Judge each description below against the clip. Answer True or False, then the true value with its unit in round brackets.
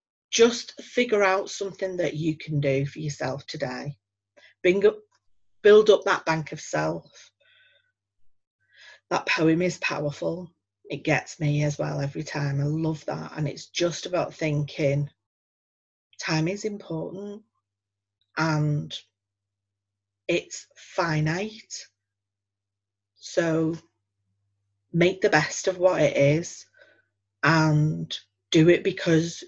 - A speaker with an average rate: False (115 wpm)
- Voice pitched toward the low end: False (155 Hz)